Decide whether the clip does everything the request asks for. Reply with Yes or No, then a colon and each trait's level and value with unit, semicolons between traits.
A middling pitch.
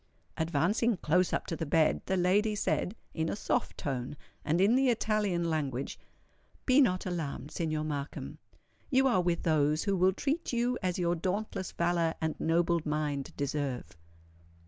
Yes: medium, 170 Hz